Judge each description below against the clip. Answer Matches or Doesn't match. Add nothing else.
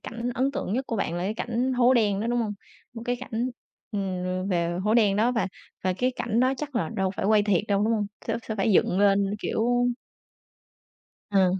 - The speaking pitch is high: Matches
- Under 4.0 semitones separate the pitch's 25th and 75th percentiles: Matches